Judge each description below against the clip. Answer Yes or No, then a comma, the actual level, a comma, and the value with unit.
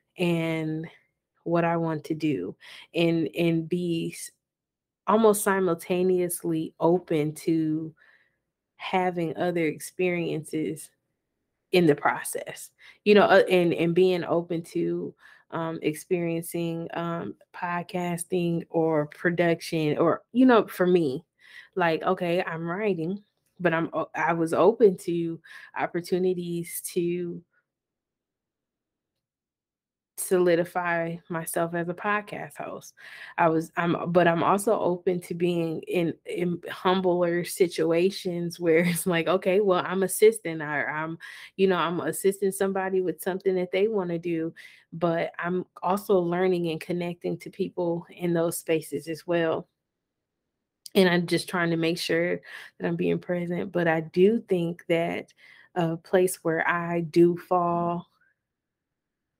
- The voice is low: No, medium, 175 Hz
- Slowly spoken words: Yes, slow, 125 wpm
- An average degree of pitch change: No, narrow, 1.7 semitones